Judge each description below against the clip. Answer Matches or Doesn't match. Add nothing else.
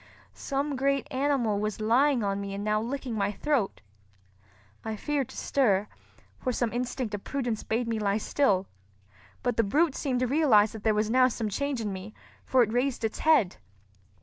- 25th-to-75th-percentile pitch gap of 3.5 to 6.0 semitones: Matches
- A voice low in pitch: Doesn't match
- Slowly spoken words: Doesn't match